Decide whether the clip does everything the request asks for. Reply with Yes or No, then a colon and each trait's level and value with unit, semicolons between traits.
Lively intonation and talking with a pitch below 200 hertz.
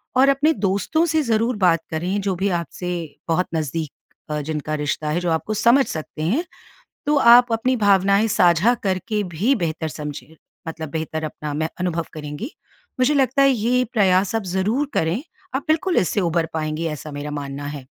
Yes: wide, 6.8 semitones; medium, 185 Hz